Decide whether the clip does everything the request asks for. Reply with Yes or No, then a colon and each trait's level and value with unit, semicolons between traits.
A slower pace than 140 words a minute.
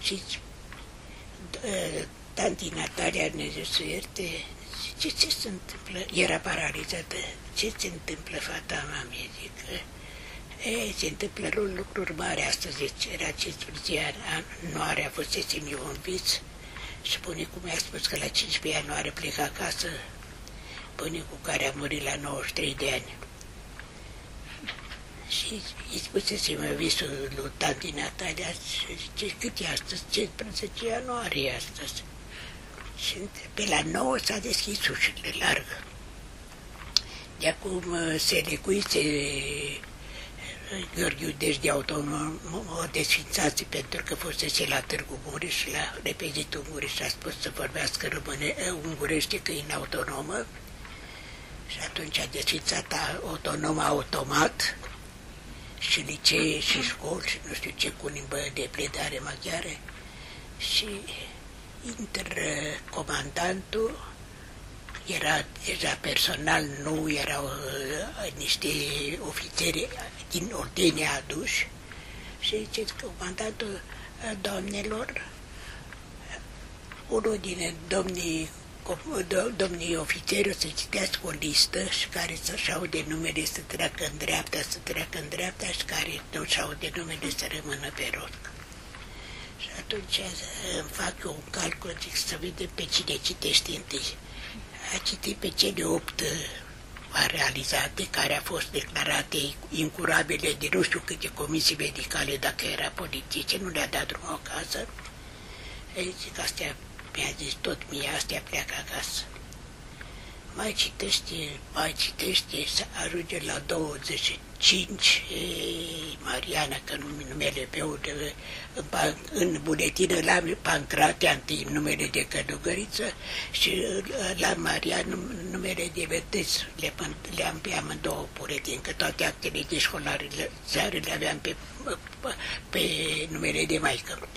Yes: average, 125 wpm